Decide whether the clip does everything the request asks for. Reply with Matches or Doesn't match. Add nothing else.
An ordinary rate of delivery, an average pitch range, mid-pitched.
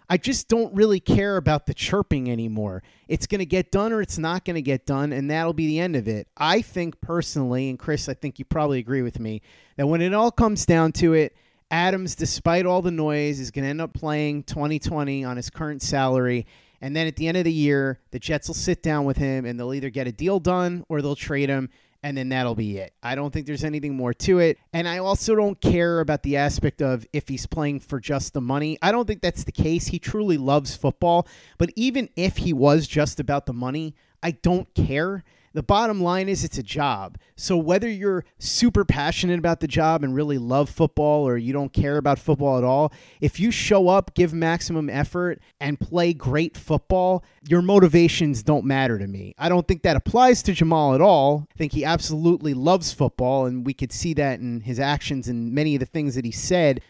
Doesn't match